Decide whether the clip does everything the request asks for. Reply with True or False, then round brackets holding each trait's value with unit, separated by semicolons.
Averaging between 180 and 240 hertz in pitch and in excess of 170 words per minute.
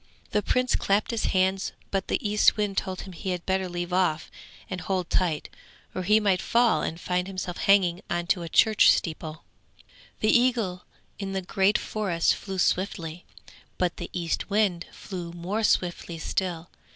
False (185 Hz; 165 wpm)